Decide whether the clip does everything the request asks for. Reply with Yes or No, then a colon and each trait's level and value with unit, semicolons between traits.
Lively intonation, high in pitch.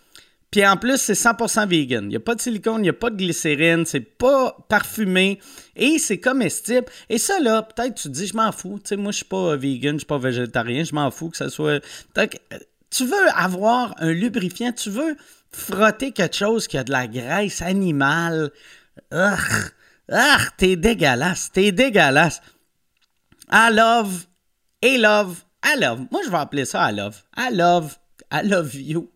Yes: wide, 6.0 semitones; high, 195 Hz